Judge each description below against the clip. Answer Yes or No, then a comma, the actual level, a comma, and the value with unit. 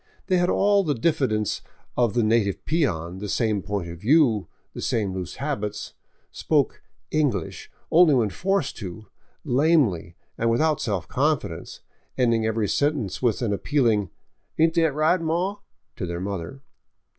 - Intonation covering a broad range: Yes, wide, 7.2 semitones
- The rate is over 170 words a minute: No, average, 155 wpm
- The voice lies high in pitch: No, low, 115 Hz